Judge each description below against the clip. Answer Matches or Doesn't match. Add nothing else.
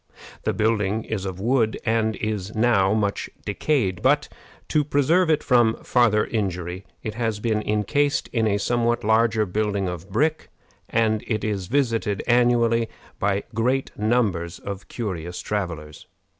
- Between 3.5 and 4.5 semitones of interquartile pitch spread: Doesn't match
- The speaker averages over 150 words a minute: Doesn't match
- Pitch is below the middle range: Matches